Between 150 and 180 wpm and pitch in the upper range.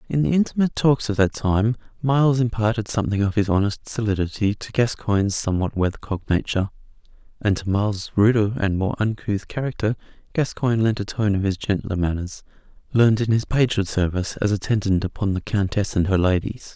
No: average, 170 wpm; low, 105 Hz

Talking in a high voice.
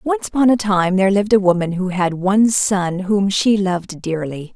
Yes: high, 195 Hz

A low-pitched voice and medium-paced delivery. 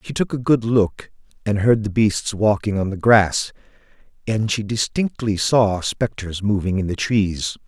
Yes: low, 105 Hz; average, 170 wpm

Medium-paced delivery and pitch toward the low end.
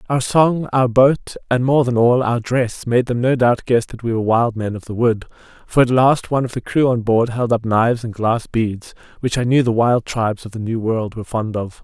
No: fast, 260 wpm; low, 120 Hz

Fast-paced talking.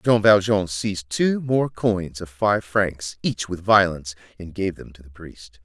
No: average, 190 wpm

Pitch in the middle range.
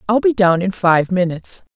No: high, 195 Hz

